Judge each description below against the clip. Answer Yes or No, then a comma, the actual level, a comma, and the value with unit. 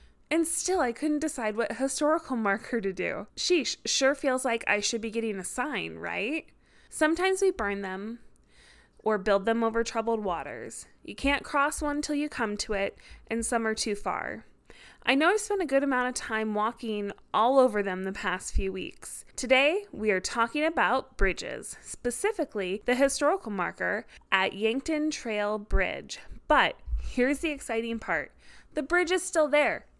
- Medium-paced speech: Yes, average, 170 wpm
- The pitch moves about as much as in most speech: No, wide, 6.1 semitones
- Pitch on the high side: Yes, high, 240 Hz